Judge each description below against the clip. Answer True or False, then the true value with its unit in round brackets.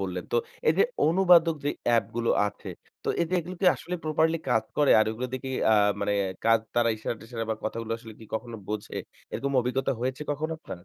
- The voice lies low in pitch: True (125 Hz)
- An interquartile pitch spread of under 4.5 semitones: False (5.5 semitones)